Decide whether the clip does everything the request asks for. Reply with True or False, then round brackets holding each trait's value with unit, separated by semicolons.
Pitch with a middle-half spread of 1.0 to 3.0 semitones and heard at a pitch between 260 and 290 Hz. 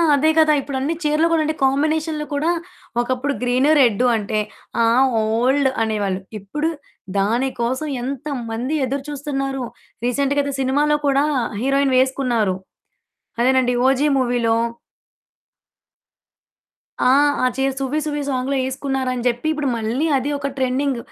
True (2.7 semitones; 270 Hz)